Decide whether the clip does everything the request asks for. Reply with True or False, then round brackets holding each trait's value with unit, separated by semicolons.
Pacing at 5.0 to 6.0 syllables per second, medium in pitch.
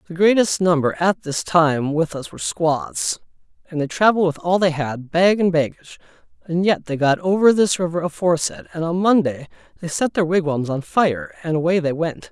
True (5.2 syllables/s; 165 Hz)